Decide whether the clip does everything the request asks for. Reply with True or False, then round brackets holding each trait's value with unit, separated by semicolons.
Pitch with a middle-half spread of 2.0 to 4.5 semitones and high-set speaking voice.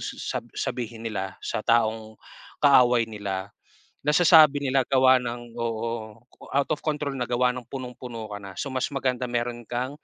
False (2.8 semitones; 120 Hz)